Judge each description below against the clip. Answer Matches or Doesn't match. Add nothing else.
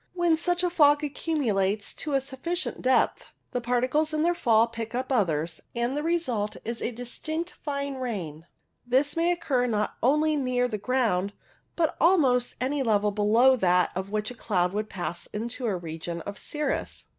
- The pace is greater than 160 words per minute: Matches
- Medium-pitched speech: Doesn't match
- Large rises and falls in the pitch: Matches